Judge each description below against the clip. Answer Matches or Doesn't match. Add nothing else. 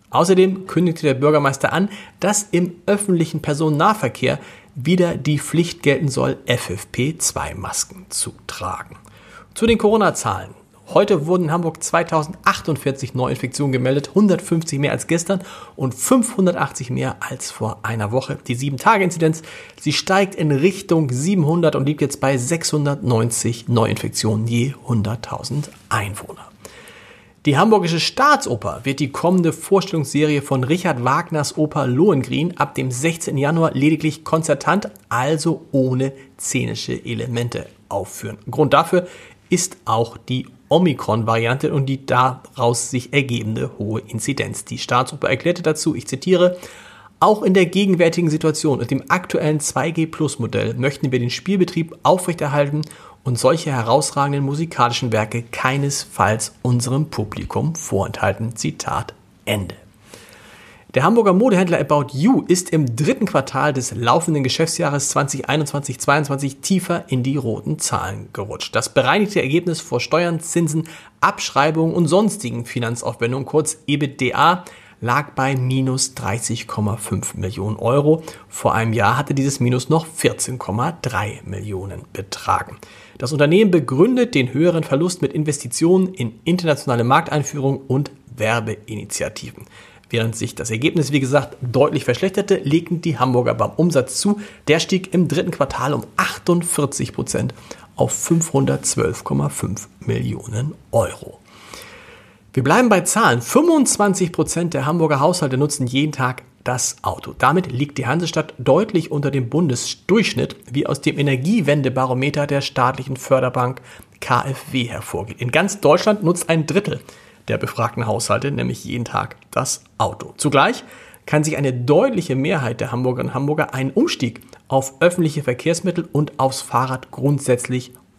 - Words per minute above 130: Doesn't match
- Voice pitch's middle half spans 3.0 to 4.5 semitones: Doesn't match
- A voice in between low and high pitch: Matches